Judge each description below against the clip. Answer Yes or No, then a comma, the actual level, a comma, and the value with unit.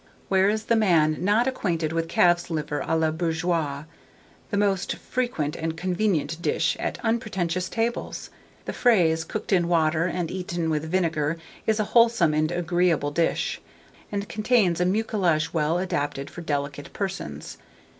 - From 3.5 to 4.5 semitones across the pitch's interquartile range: Yes, average, 4.1 semitones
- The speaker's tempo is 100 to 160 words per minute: Yes, average, 150 wpm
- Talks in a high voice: No, medium, 175 Hz